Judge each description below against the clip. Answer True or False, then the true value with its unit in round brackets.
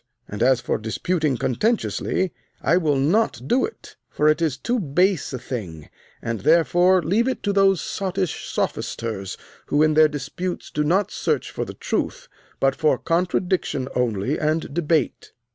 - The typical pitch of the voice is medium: True (155 Hz)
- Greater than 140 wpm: True (160 wpm)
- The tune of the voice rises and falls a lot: True (5.7 semitones)